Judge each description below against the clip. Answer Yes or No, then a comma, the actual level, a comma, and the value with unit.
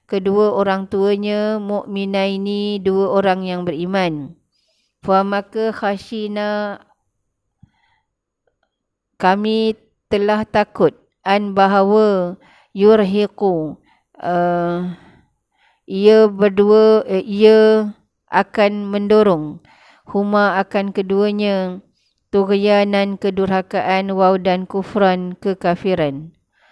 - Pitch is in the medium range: No, high, 200 Hz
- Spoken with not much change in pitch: Yes, narrow, 1.6 semitones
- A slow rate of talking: Yes, slow, 70 wpm